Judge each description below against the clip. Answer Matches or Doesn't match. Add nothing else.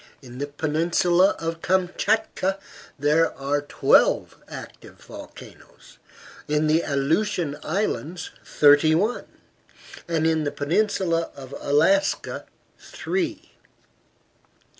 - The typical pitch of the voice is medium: Matches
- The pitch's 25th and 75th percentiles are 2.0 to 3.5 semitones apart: Doesn't match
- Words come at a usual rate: Doesn't match